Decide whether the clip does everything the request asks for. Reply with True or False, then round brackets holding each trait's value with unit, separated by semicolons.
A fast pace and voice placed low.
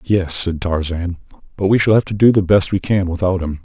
True (245 wpm; 90 Hz)